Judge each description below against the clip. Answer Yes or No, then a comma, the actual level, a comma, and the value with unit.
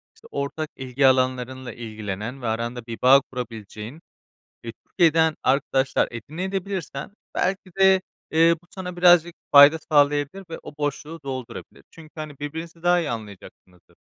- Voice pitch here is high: No, medium, 145 Hz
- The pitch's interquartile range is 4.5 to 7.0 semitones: Yes, average, 5.1 semitones